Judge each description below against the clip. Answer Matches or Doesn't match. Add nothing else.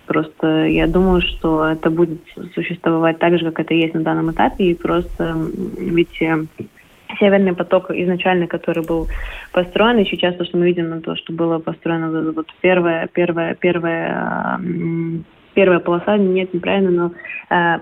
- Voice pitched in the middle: Matches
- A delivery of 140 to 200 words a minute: Matches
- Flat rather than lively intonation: Matches